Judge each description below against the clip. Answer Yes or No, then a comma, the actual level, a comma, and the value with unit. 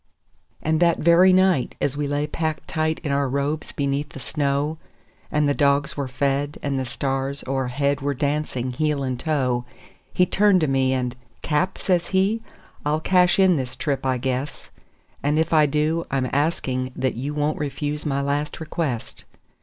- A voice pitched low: No, medium, 145 Hz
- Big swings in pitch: No, narrow, 2.6 semitones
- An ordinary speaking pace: Yes, average, 175 wpm